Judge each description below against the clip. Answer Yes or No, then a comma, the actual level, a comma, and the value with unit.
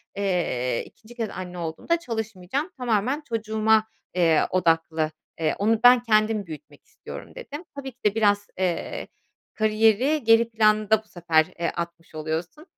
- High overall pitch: Yes, high, 215 Hz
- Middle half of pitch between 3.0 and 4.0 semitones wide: No, average, 4.8 semitones